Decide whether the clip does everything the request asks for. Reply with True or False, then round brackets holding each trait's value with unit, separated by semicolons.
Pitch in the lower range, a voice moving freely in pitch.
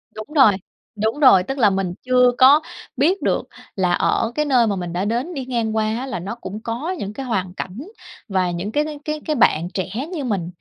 False (225 Hz; 5.8 semitones)